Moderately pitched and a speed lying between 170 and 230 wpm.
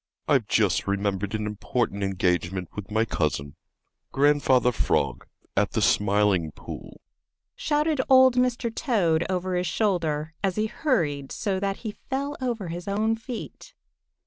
No: medium, 165 Hz; average, 140 wpm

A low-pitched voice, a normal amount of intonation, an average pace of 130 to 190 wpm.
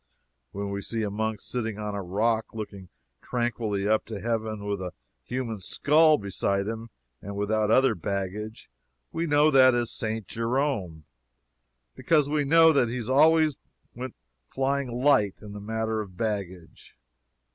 Yes: low, 110 Hz; average, 4.3 semitones; average, 155 wpm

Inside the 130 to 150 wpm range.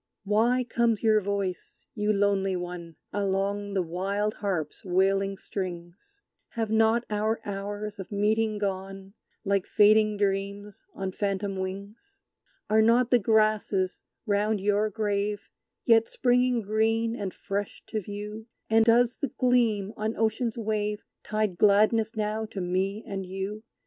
Yes: slow, 135 wpm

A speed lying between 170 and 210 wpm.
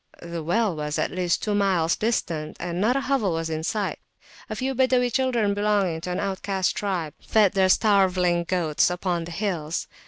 Yes: average, 185 wpm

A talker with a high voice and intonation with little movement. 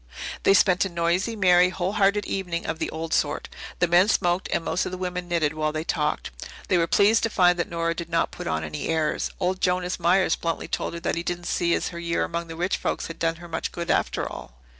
No: medium, 175 Hz; narrow, 1.7 semitones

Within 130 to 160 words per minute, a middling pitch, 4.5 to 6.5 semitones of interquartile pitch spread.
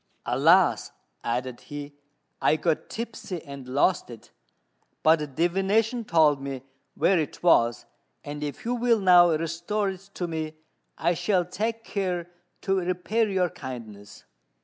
Yes: slow, 135 wpm; medium, 170 Hz; average, 4.9 semitones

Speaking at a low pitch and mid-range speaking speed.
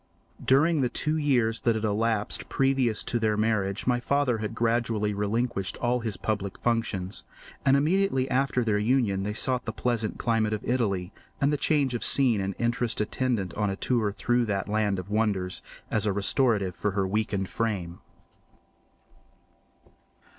Yes: low, 110 Hz; average, 160 wpm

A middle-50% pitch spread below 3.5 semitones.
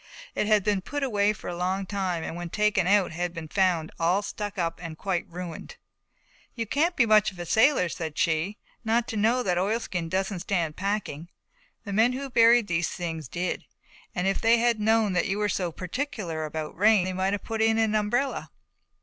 No: average, 4.0 semitones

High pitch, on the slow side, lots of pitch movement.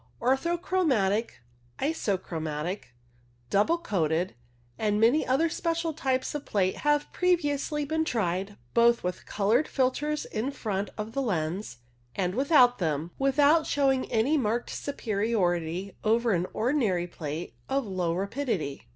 Yes: high, 230 Hz; slow, 125 wpm; wide, 7.3 semitones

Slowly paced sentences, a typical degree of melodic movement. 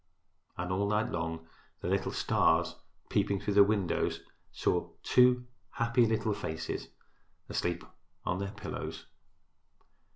Yes: slow, 120 wpm; average, 3.9 semitones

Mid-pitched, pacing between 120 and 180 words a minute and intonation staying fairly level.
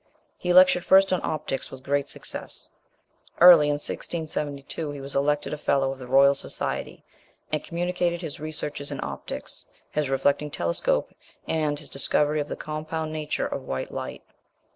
Yes: medium, 150 Hz; average, 160 wpm; narrow, 2.3 semitones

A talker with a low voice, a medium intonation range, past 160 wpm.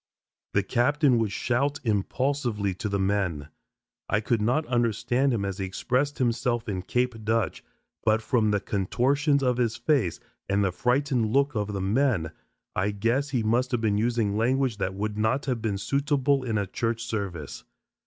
Yes: low, 115 Hz; average, 4.0 semitones; average, 175 wpm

